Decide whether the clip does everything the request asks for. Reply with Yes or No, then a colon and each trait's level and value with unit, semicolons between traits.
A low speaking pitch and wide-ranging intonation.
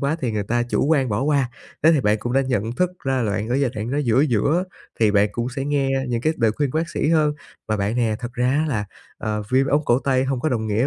No: low, 125 Hz; average, 4.1 semitones